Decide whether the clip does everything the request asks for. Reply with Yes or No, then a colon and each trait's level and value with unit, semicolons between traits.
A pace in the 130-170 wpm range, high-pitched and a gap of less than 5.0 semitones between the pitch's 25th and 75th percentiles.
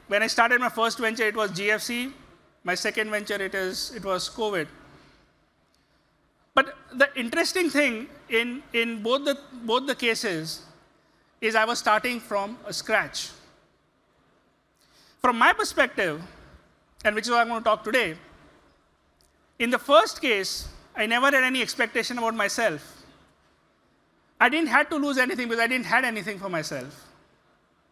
Yes: average, 155 wpm; high, 235 Hz; average, 3.4 semitones